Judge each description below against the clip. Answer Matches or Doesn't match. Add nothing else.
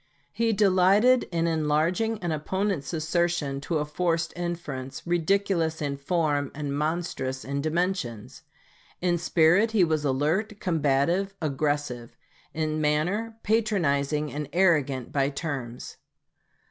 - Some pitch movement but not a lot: Matches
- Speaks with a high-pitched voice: Doesn't match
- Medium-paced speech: Doesn't match